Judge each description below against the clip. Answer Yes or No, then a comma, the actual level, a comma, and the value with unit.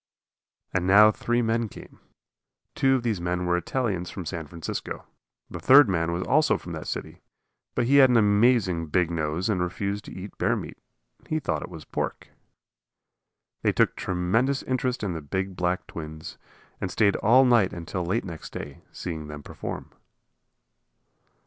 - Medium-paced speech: Yes, average, 170 wpm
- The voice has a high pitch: No, very low, 95 Hz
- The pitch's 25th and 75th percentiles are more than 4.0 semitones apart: Yes, wide, 5.4 semitones